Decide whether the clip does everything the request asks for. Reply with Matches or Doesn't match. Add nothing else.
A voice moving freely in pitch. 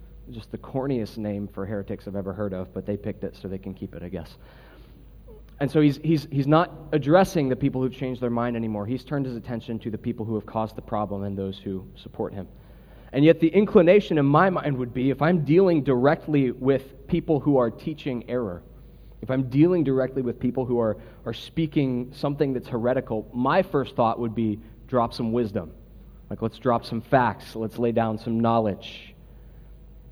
Doesn't match